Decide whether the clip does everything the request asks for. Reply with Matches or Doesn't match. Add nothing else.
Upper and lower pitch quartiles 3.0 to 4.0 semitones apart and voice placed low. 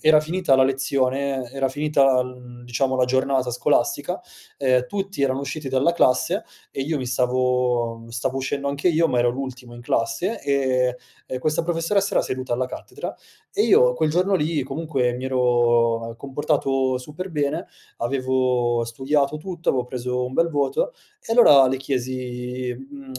Doesn't match